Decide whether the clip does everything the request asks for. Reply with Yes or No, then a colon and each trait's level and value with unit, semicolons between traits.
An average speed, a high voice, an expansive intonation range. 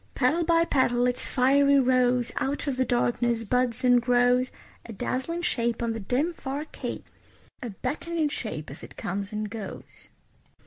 No: average, 165 wpm; very high, 250 Hz; average, 3.0 semitones